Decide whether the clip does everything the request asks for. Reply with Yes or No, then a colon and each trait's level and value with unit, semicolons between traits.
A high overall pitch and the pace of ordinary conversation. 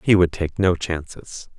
No: very low, 85 Hz; average, 190 wpm